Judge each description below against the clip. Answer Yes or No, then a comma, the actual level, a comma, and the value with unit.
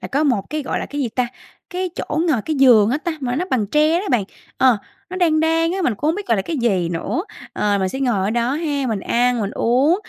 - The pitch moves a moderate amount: No, wide, 5.7 semitones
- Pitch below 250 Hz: No, very high, 260 Hz